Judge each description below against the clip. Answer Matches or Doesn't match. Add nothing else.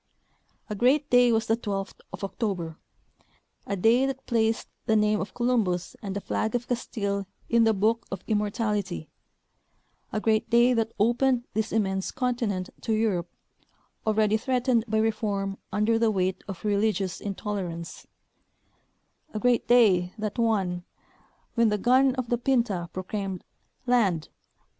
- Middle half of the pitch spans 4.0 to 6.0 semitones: Doesn't match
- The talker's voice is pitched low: Doesn't match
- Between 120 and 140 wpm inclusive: Doesn't match